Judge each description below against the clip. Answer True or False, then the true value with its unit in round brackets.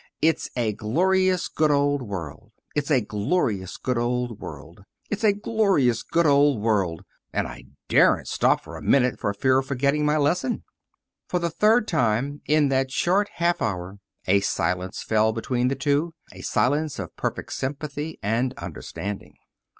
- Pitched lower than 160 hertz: True (135 Hz)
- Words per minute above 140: True (160 wpm)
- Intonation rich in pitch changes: True (6.4 semitones)